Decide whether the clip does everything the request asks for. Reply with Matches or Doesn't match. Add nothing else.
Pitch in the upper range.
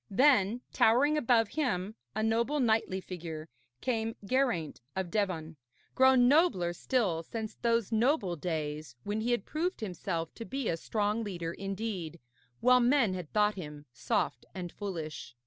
Matches